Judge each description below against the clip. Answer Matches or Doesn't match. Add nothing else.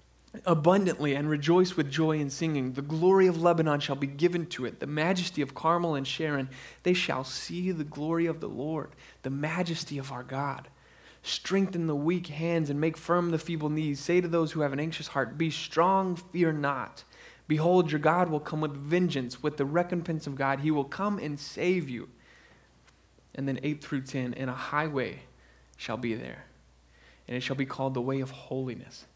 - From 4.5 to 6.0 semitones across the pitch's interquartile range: Doesn't match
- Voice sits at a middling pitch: Matches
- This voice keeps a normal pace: Matches